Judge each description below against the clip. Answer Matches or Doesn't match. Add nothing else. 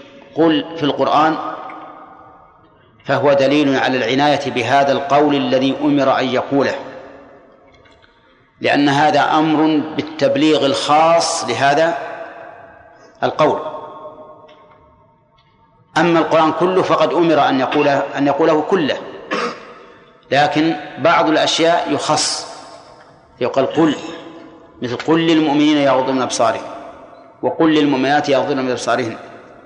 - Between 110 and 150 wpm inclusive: Doesn't match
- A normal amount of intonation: Doesn't match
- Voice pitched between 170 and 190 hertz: Doesn't match